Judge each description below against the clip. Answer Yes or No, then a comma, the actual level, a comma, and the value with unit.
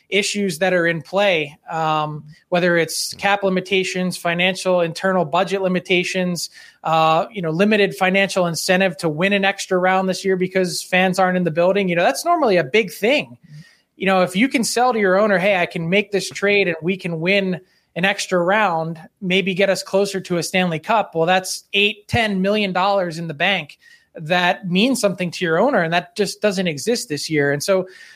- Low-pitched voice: No, medium, 185 Hz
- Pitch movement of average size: No, narrow, 2.2 semitones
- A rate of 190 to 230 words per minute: Yes, average, 200 wpm